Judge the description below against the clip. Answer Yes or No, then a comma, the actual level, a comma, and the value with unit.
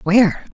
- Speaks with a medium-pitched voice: No, high, 195 Hz